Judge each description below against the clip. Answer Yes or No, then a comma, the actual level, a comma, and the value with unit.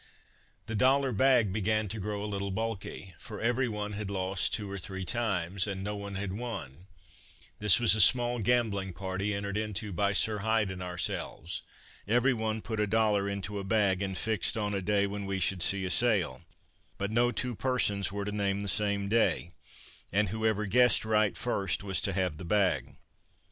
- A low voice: Yes, low, 100 Hz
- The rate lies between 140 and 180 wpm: No, average, 190 wpm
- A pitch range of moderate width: No, narrow, 2.3 semitones